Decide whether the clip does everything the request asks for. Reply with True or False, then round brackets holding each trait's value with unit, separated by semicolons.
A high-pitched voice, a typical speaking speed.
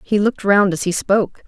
False (200 Hz; 245 wpm)